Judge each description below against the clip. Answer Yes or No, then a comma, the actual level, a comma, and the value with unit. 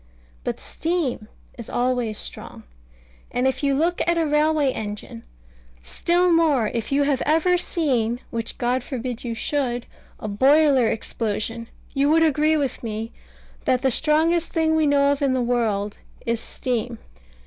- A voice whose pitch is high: Yes, very high, 265 Hz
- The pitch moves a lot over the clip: No, average, 4.9 semitones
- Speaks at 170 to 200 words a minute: No, average, 155 wpm